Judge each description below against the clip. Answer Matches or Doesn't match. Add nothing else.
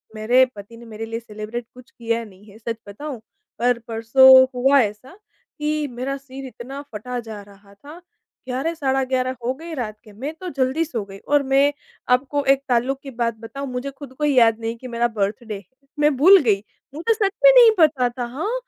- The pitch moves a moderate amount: Matches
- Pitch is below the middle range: Doesn't match